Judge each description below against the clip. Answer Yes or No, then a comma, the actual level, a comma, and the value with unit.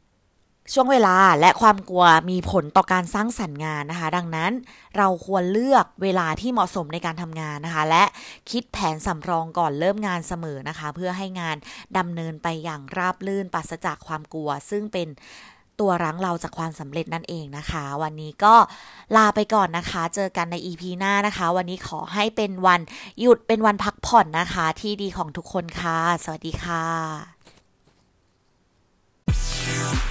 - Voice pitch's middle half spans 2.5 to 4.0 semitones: Yes, average, 3.6 semitones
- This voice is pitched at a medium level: Yes, medium, 180 Hz